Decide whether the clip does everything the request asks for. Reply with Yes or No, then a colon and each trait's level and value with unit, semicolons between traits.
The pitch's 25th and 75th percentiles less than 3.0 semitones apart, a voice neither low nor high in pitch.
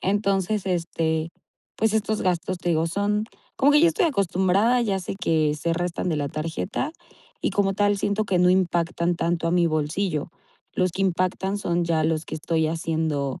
No: average, 3.4 semitones; medium, 180 Hz